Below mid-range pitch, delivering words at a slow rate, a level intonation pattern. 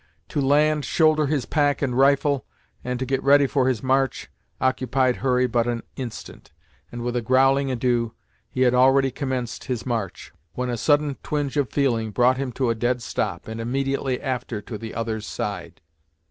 No: low, 130 Hz; average, 180 wpm; narrow, 2.3 semitones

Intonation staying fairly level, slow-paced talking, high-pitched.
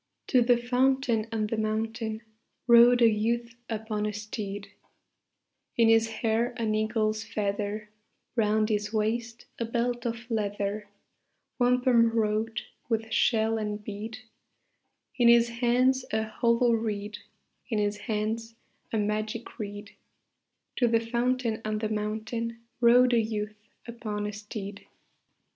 Yes: narrow, 1.7 semitones; slow, 130 wpm; high, 225 Hz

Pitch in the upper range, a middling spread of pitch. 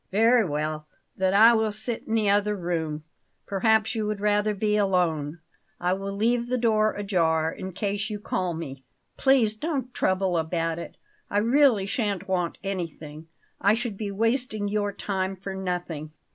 Yes: high, 200 Hz; average, 3.7 semitones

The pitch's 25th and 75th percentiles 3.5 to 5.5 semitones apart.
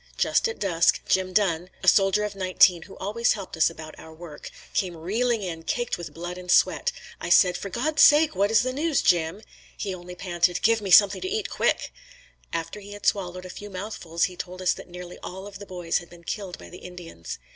No: average, 2.9 semitones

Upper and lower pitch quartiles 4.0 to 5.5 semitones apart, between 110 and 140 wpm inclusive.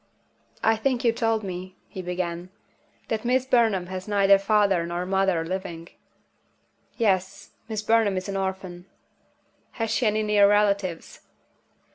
No: average, 2.9 semitones; slow, 135 wpm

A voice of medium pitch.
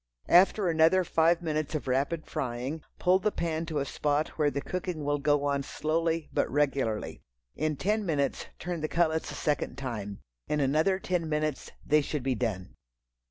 Yes: medium, 155 Hz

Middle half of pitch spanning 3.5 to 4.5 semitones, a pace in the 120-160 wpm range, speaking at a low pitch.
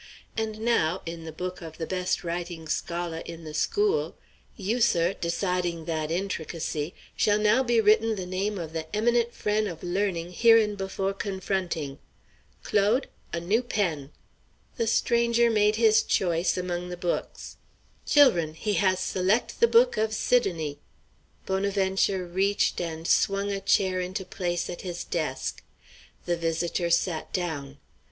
No: average, 3.9 semitones; average, 145 wpm; medium, 185 Hz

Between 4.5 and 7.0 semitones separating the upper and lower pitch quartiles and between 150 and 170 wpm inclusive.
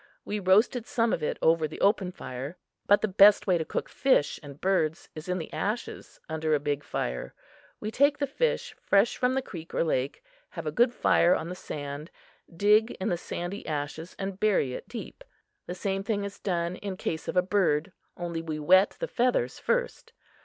No: average, 4.8 semitones; average, 200 wpm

